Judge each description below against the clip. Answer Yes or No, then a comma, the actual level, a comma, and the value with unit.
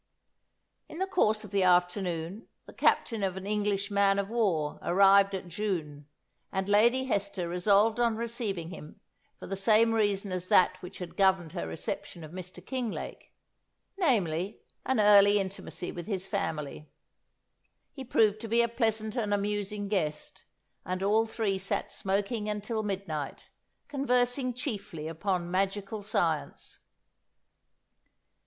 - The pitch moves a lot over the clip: No, average, 3.1 semitones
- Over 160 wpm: No, average, 140 wpm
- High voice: Yes, high, 200 Hz